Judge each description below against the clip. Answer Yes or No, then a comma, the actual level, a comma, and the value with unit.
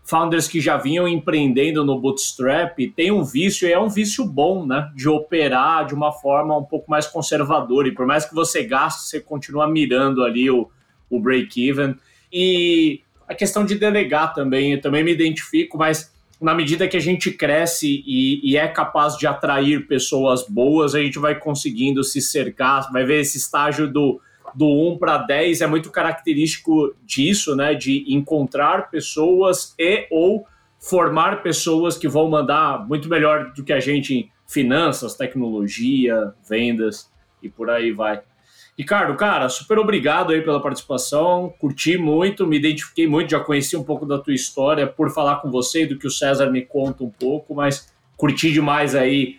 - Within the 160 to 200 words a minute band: Yes, average, 175 wpm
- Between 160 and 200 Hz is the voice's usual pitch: No, medium, 150 Hz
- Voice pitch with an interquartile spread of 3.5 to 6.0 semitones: No, average, 3.0 semitones